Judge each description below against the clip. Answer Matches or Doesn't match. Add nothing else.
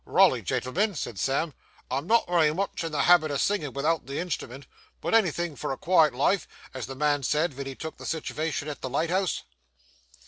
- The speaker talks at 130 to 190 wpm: Doesn't match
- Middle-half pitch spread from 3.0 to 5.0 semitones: Matches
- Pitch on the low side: Doesn't match